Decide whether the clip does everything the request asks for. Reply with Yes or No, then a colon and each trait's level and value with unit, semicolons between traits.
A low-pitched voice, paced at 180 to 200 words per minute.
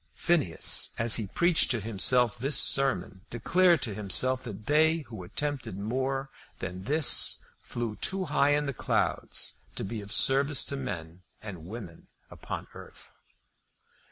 No: low, 125 Hz; average, 145 wpm